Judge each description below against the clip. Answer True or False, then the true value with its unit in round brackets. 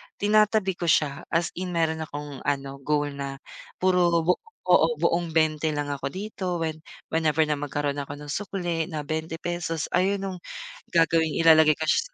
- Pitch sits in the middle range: True (160 Hz)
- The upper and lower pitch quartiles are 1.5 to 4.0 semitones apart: True (3.1 semitones)